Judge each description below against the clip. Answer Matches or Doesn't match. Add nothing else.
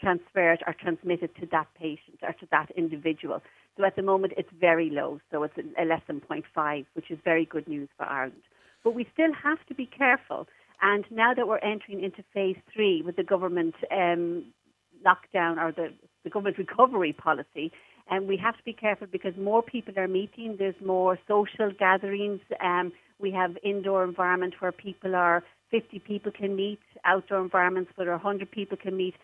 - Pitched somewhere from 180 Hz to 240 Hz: Matches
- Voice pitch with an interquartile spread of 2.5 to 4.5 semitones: Matches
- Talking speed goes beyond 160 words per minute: Matches